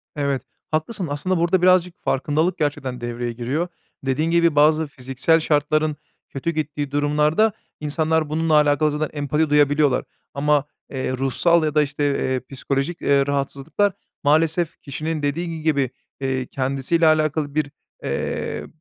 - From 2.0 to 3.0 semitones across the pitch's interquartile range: Yes, narrow, 2.4 semitones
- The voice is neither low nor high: Yes, medium, 150 Hz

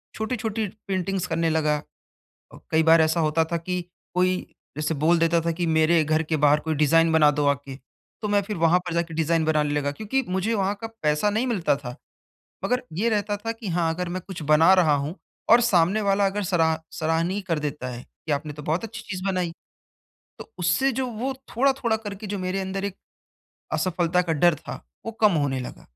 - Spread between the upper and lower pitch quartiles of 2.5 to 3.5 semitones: No, average, 4.3 semitones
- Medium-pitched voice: Yes, medium, 175 Hz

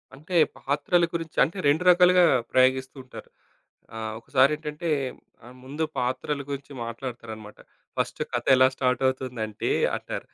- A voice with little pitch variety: No, average, 3.2 semitones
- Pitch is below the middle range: Yes, low, 130 Hz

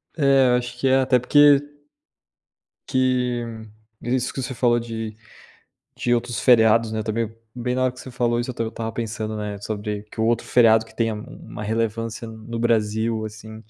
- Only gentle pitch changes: Yes, narrow, 2.1 semitones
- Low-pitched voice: Yes, low, 115 Hz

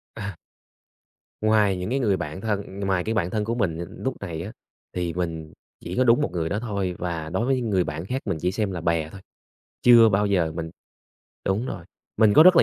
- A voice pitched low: Yes, very low, 95 Hz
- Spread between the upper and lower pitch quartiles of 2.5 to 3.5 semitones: No, average, 4.3 semitones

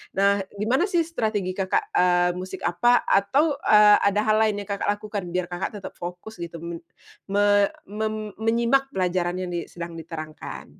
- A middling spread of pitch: Yes, average, 3.5 semitones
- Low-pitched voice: No, high, 200 Hz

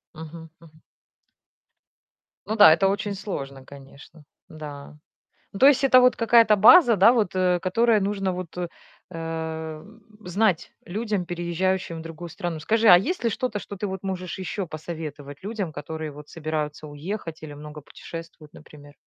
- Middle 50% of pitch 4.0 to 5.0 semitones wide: Yes, average, 4.6 semitones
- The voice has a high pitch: No, medium, 175 Hz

